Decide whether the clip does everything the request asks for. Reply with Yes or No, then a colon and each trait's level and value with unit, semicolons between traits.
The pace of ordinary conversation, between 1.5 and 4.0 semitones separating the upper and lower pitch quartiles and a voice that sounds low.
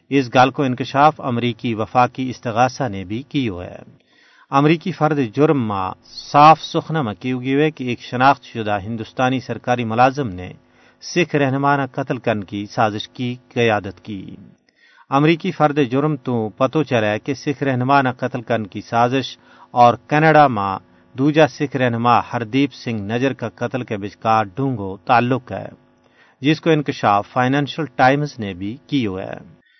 Yes: average, 145 wpm; average, 3.7 semitones; low, 125 Hz